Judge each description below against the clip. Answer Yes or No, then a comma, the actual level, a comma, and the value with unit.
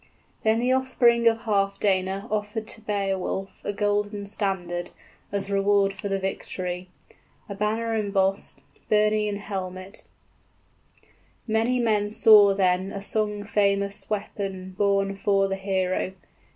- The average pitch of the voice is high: Yes, high, 200 Hz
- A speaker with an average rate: No, slow, 130 wpm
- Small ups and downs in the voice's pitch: Yes, narrow, 1.5 semitones